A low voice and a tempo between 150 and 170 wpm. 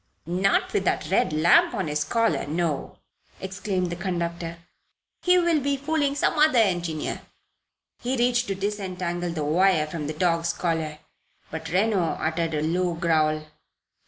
No: medium, 175 Hz; average, 155 wpm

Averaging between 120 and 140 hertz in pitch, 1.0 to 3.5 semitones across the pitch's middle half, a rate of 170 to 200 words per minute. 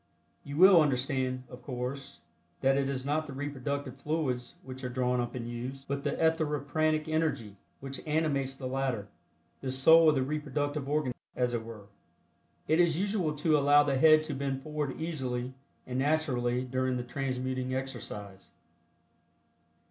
No: low, 135 Hz; average, 3.0 semitones; average, 155 wpm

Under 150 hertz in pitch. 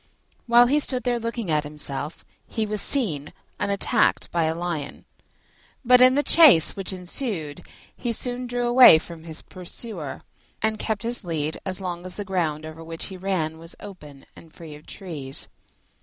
No: medium, 185 Hz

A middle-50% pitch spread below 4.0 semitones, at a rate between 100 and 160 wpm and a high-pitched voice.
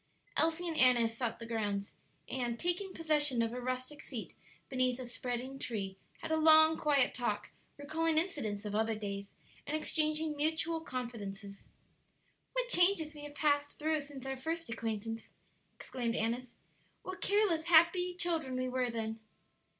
No: wide, 5.5 semitones; average, 155 wpm; very high, 265 Hz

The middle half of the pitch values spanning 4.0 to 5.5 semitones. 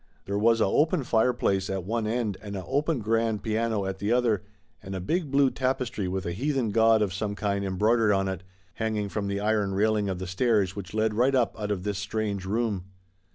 No: average, 2.9 semitones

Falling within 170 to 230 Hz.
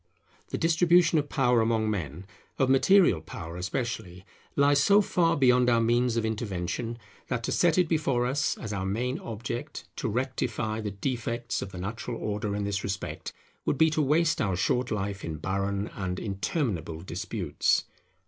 No: low, 115 Hz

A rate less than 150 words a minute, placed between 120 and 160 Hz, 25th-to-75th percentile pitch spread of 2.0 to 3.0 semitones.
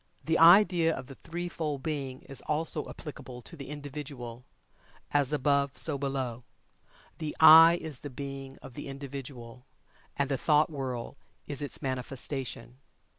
Yes: average, 140 wpm; medium, 140 Hz; narrow, 2.5 semitones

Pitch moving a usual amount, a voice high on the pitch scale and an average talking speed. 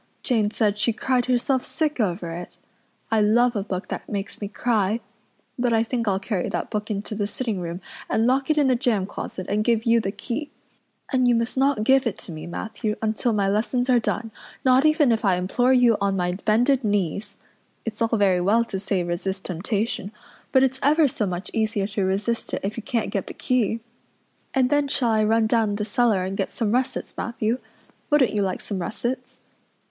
No: average, 3.6 semitones; high, 220 Hz; fast, 210 wpm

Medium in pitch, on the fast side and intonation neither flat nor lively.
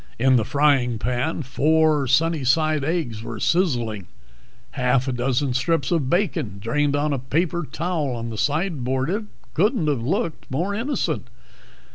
No: medium, 145 Hz; average, 145 wpm; average, 4.6 semitones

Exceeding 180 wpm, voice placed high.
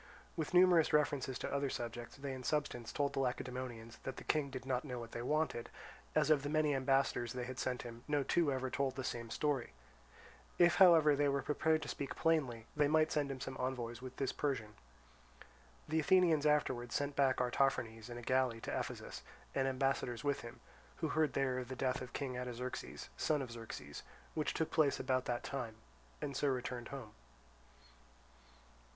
No: average, 190 wpm; low, 135 Hz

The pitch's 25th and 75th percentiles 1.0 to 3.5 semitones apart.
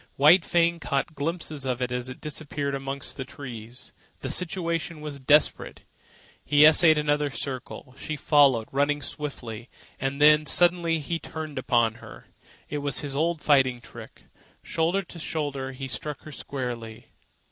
Yes: average, 2.7 semitones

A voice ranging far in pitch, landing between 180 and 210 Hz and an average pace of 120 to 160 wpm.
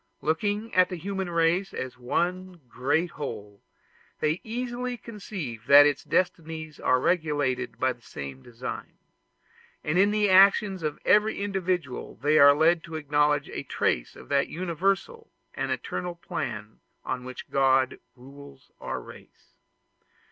No: wide, 5.9 semitones; medium, 160 Hz; average, 140 wpm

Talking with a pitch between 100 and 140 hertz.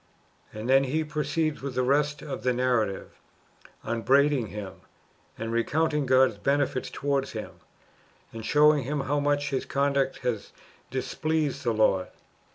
Yes: low, 135 Hz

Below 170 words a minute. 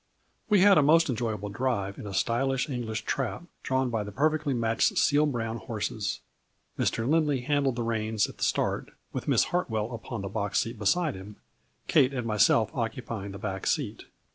No: average, 185 wpm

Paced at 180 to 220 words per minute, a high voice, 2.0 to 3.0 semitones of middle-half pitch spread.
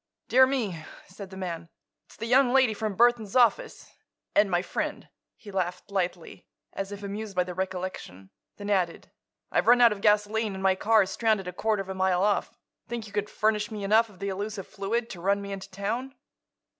Yes: average, 200 wpm; high, 200 Hz; average, 2.7 semitones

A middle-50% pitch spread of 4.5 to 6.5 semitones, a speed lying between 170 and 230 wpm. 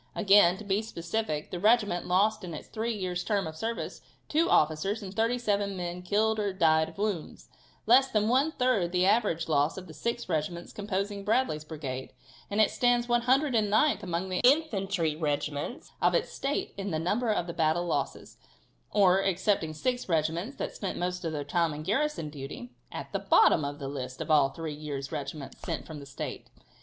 Yes: wide, 5.5 semitones; average, 190 wpm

